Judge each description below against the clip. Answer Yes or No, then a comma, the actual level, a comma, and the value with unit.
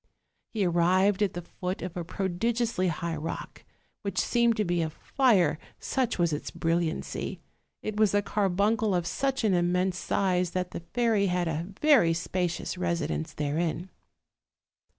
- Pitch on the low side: No, medium, 180 Hz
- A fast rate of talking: No, average, 150 wpm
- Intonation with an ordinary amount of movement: Yes, average, 3.4 semitones